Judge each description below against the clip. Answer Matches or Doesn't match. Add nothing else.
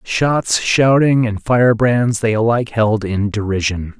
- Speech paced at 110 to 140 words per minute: Matches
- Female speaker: Doesn't match